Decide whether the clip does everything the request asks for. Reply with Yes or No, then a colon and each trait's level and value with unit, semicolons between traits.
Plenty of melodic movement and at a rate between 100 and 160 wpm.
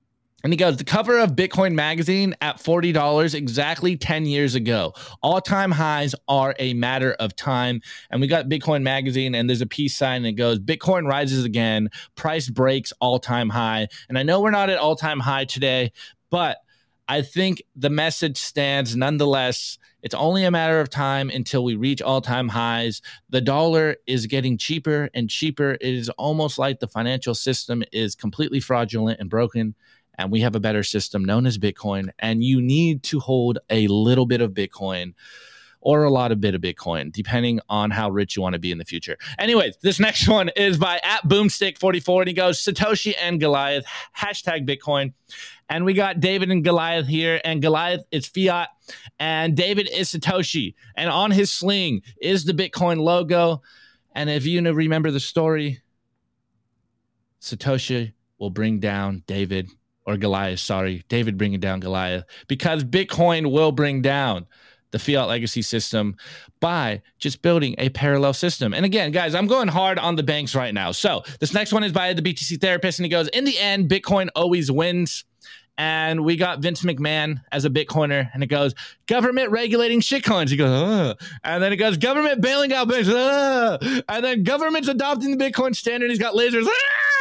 No: wide, 6.7 semitones; average, 185 wpm